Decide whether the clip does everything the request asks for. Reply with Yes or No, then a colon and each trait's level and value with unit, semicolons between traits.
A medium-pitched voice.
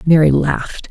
Yes: medium, 160 Hz